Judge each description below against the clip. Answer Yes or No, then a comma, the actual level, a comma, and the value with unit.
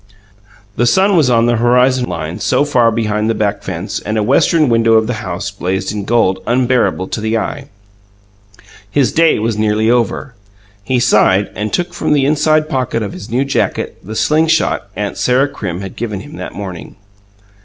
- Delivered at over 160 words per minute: Yes, average, 185 wpm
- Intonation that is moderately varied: Yes, average, 4.1 semitones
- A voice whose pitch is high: No, low, 115 Hz